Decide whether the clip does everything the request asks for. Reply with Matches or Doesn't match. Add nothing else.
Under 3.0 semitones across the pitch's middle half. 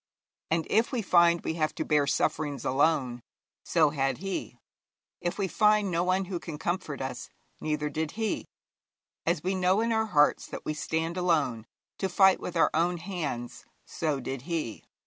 Doesn't match